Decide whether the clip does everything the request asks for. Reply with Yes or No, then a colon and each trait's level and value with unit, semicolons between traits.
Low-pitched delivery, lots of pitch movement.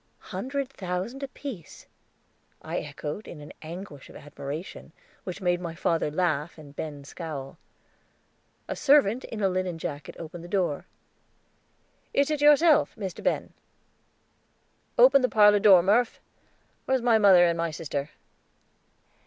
No: medium, 180 Hz; wide, 6.5 semitones